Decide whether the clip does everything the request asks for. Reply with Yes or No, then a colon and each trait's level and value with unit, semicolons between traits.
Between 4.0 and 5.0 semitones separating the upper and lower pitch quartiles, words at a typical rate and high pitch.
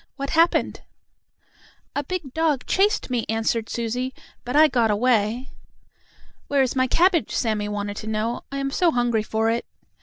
Yes: average, 4.3 semitones; average, 160 wpm; very high, 250 Hz